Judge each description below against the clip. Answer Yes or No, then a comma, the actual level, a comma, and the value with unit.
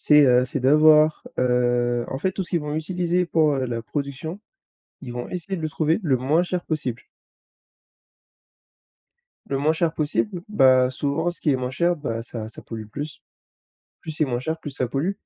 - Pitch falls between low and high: Yes, medium, 145 Hz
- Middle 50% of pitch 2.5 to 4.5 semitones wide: Yes, average, 4.1 semitones